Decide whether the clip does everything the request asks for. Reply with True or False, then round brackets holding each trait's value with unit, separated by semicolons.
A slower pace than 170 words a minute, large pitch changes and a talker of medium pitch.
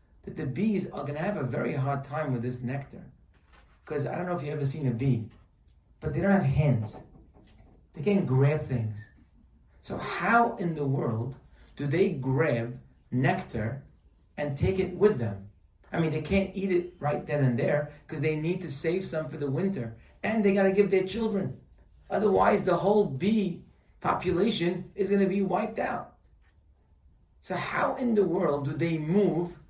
False (180 wpm; 7.2 semitones; 155 Hz)